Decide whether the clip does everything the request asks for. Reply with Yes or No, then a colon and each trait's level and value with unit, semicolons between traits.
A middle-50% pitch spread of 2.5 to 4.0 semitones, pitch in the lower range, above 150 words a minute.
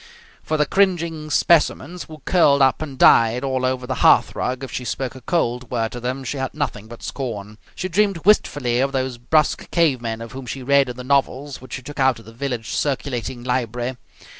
Yes: average, 3.2 semitones; low, 130 Hz; fast, 205 wpm